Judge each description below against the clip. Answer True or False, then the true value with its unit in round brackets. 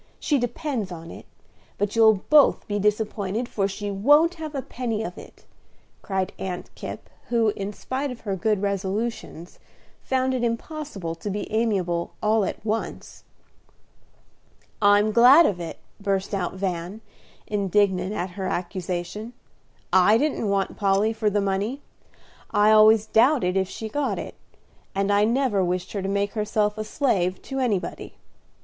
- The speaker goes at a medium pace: True (155 wpm)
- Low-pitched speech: False (210 Hz)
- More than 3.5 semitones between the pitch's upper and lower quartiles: False (3.2 semitones)